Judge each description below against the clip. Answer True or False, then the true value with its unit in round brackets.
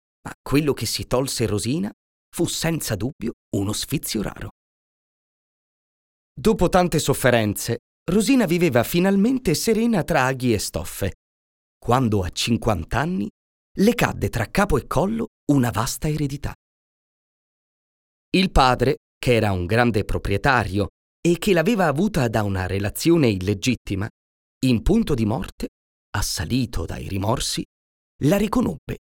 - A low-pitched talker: True (120 Hz)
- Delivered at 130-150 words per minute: False (120 wpm)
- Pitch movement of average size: False (8.5 semitones)